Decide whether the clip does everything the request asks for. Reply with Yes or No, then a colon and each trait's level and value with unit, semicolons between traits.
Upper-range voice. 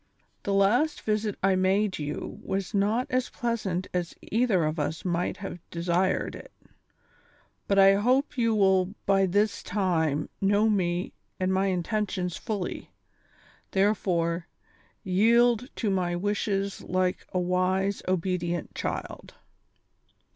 Yes: high, 195 Hz